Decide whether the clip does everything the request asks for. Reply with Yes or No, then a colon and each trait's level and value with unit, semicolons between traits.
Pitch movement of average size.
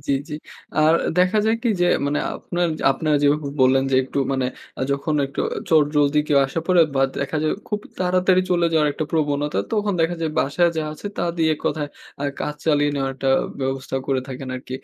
Yes: average, 3.4 semitones